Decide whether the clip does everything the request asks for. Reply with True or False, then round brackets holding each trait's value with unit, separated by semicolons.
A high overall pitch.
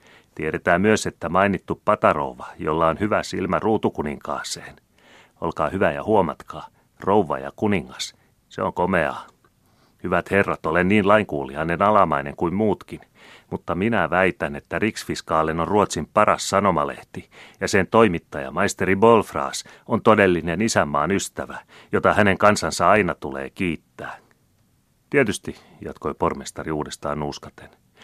False (95 Hz)